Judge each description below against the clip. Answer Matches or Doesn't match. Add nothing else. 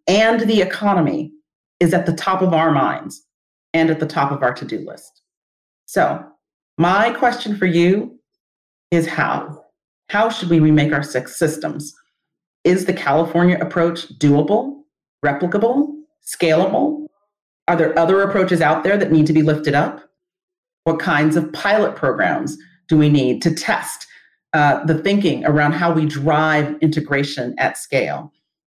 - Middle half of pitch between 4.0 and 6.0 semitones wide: Matches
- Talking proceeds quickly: Doesn't match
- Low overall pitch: Doesn't match